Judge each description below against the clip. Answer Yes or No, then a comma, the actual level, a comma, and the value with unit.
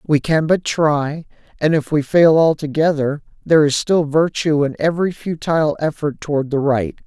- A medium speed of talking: Yes, average, 170 wpm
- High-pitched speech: No, medium, 155 Hz